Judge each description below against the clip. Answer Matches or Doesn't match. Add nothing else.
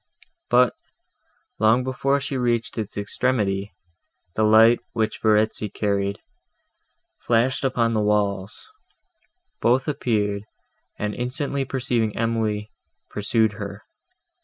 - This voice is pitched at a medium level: Doesn't match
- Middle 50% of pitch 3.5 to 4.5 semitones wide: Doesn't match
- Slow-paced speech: Matches